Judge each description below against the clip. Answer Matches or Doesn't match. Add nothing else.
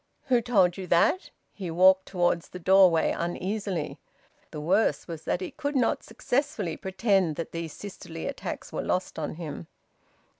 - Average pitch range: Matches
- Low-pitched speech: Doesn't match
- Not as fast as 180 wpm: Matches